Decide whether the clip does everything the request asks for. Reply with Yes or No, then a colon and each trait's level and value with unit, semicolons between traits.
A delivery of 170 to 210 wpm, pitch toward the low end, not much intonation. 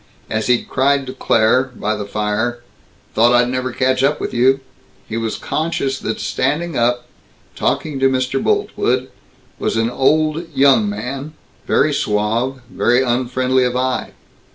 No: average, 150 wpm; low, 130 Hz; narrow, 2.1 semitones